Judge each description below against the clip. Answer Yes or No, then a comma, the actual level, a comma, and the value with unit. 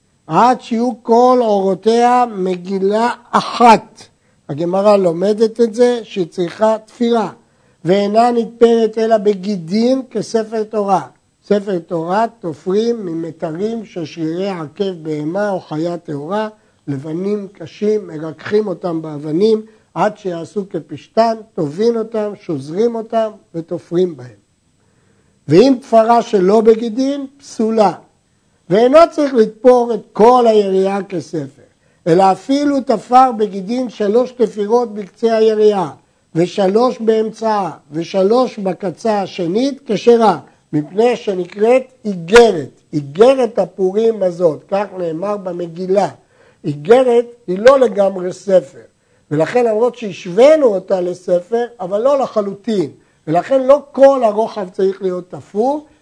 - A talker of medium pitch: No, high, 210 Hz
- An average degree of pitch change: Yes, average, 4.3 semitones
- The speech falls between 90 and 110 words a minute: Yes, average, 105 wpm